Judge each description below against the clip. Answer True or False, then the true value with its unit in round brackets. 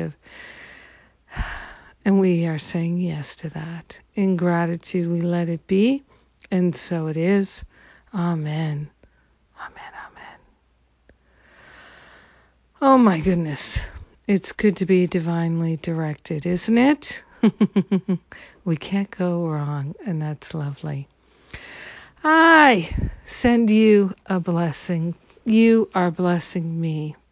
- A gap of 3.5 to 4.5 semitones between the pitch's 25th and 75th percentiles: True (3.8 semitones)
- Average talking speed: False (105 wpm)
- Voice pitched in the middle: True (175 Hz)